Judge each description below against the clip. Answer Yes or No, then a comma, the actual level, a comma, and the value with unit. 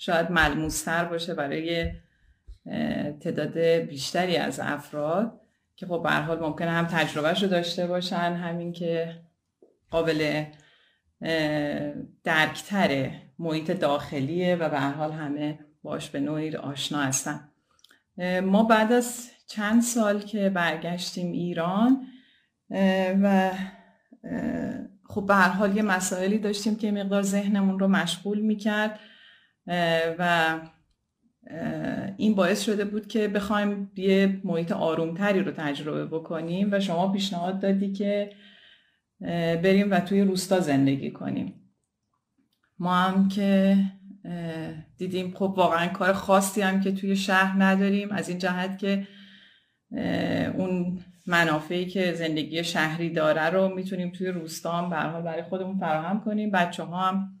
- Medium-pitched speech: Yes, medium, 180 Hz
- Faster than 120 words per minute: No, average, 115 wpm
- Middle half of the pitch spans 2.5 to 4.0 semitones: Yes, average, 3.3 semitones